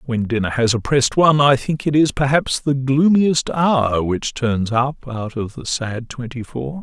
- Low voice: Yes, low, 130 Hz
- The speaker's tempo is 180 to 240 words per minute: Yes, average, 195 wpm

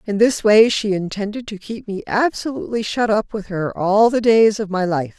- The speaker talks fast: Yes, fast, 220 wpm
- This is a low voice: No, high, 210 Hz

